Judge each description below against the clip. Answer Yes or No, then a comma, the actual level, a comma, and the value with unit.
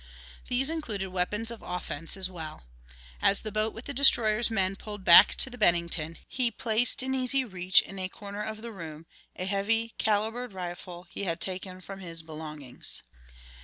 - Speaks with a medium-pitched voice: No, high, 195 Hz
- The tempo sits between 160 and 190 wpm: Yes, average, 175 wpm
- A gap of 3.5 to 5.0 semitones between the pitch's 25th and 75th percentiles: Yes, average, 4.1 semitones